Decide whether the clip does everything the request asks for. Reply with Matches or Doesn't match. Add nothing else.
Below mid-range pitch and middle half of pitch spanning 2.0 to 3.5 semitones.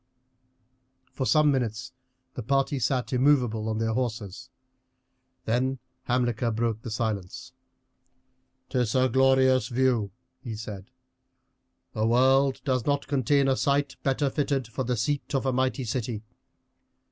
Matches